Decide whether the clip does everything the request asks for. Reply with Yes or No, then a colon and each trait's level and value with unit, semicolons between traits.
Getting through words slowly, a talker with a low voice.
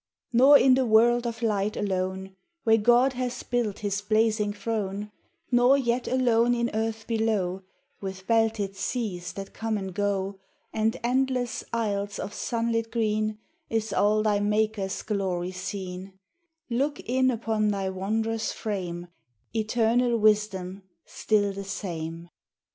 No: slow, 130 wpm; high, 215 Hz